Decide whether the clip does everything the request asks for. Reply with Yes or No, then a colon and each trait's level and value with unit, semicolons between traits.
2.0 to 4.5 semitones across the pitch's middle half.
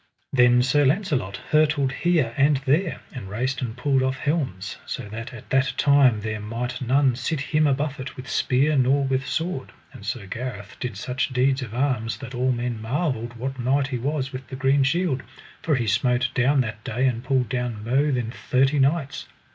Yes: narrow, 2.5 semitones